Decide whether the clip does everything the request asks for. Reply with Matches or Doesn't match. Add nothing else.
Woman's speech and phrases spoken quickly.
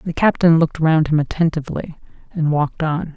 Doesn't match